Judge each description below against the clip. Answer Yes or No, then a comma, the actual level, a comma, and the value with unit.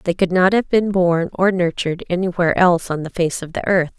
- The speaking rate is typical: No, fast, 240 wpm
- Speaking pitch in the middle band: Yes, medium, 180 Hz